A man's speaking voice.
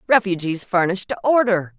No: female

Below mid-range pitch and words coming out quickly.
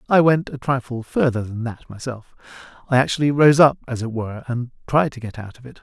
Yes: low, 125 Hz; fast, 225 wpm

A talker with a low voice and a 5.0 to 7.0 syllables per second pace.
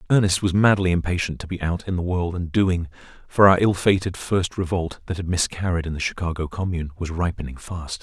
Yes: very low, 90 Hz; 5.7 syllables/s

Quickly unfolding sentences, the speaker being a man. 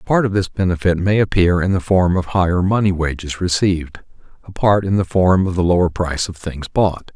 Yes: fast, 225 wpm; male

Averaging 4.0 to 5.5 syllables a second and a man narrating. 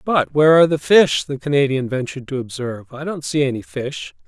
No: 5.9 syllables/s; male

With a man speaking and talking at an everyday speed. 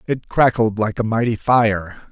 Yes: male; average, 170 wpm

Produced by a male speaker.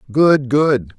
Yes: male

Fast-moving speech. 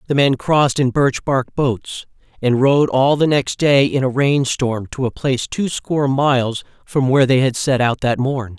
Yes: fast, 215 wpm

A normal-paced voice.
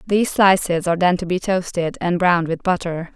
No: fast, 210 wpm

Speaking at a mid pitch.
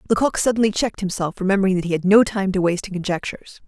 No: high, 195 Hz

